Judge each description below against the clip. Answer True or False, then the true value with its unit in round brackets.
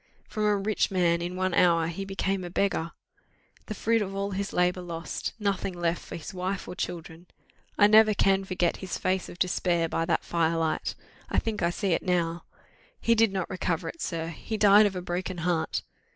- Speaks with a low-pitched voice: False (185 Hz)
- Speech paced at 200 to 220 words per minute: True (205 wpm)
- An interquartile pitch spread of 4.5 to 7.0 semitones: False (2.6 semitones)